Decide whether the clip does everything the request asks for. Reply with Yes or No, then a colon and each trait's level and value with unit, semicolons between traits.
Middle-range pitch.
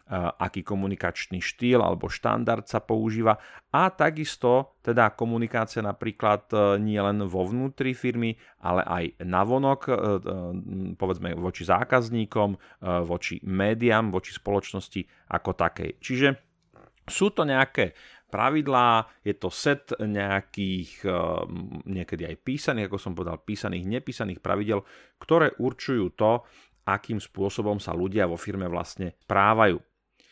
No: low, 105 Hz